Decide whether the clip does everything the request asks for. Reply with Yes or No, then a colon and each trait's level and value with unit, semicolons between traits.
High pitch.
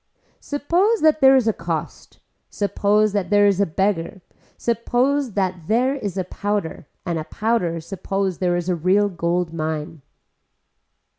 Yes: high, 195 Hz